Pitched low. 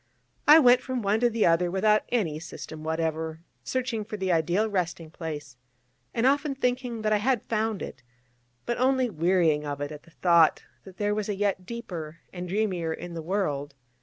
No: high, 190 Hz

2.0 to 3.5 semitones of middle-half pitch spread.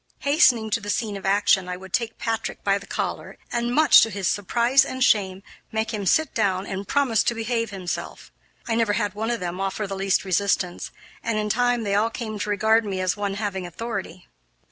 Yes: average, 2.9 semitones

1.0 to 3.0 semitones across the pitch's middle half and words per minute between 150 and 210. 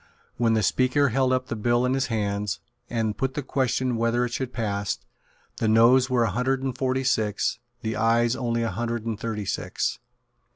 Yes: narrow, 2.5 semitones; average, 195 wpm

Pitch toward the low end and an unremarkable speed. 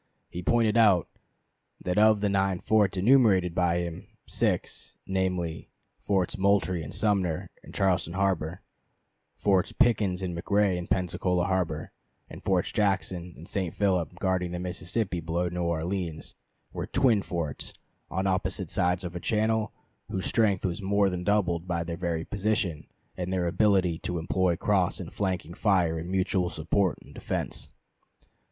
Yes: very low, 90 Hz; average, 150 wpm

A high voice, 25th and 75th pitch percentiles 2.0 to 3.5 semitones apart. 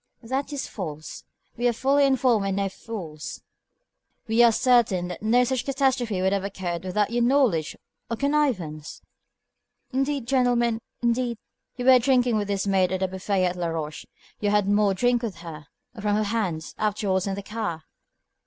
No: high, 210 Hz; average, 4.7 semitones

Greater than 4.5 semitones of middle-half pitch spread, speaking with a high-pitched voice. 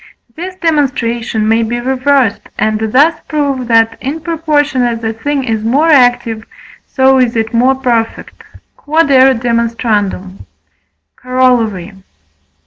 No: average, 3.8 semitones; very high, 250 Hz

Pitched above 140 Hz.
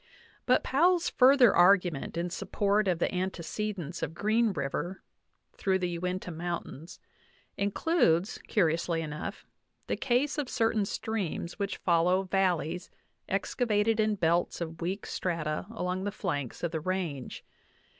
Yes: medium, 185 Hz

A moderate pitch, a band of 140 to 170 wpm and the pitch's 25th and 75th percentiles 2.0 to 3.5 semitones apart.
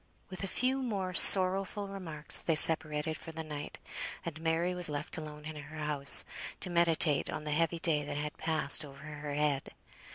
No: medium, 155 Hz; average, 185 wpm; average, 2.7 semitones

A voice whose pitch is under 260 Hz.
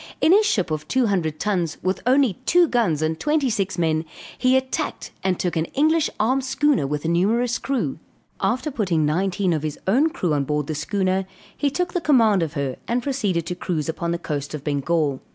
Yes: high, 190 Hz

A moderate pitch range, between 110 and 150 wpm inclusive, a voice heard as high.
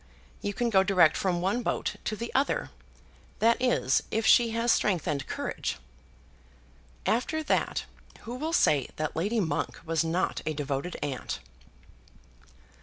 No: wide, 6.7 semitones; average, 145 wpm; high, 195 Hz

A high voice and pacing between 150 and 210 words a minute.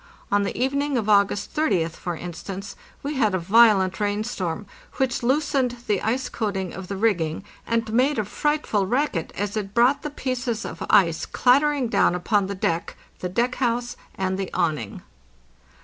Yes: high, 215 Hz; average, 180 wpm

